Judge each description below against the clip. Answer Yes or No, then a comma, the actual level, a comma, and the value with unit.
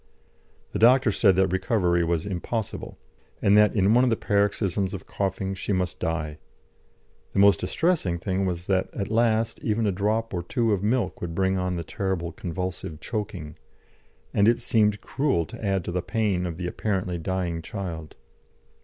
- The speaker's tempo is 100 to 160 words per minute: No, average, 175 wpm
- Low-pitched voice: Yes, very low, 95 Hz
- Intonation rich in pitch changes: No, average, 3.3 semitones